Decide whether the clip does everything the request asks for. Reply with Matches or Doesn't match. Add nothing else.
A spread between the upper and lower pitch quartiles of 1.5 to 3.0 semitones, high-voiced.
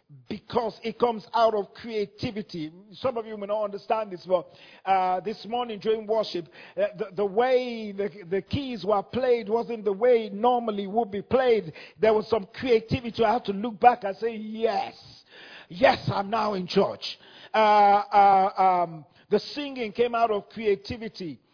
Matches